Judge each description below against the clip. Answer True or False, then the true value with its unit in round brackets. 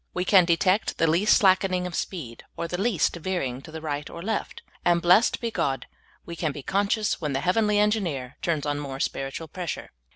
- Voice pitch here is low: False (170 Hz)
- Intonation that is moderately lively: True (4.7 semitones)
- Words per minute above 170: True (200 wpm)